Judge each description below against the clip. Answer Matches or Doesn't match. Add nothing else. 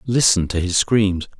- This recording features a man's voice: Matches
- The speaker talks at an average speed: Matches